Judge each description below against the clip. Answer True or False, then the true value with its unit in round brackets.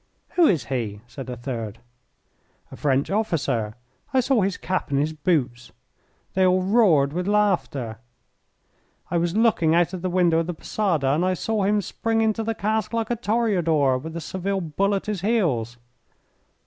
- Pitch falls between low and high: True (175 Hz)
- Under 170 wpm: False (175 wpm)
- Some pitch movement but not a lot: False (6.9 semitones)